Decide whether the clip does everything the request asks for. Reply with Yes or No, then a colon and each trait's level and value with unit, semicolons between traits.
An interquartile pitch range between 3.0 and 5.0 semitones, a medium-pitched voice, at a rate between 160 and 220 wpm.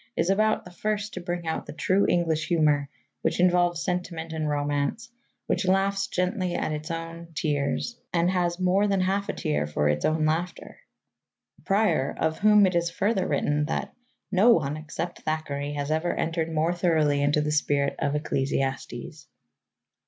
Yes: average, 3.5 semitones; medium, 165 Hz; average, 165 wpm